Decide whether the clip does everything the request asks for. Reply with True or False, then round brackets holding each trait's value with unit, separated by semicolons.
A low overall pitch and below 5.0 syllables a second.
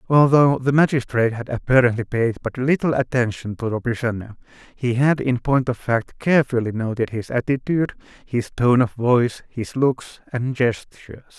False (125 Hz; 5.1 syllables/s)